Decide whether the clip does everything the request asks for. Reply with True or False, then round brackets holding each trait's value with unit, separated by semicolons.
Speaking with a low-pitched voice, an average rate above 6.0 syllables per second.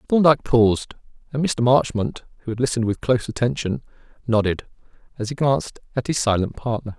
True (120 Hz; 6.2 syllables/s)